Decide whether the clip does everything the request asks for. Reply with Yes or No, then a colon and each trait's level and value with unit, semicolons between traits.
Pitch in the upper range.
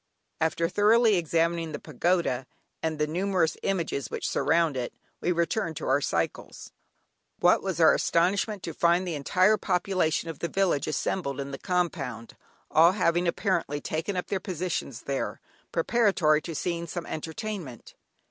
No: medium, 170 Hz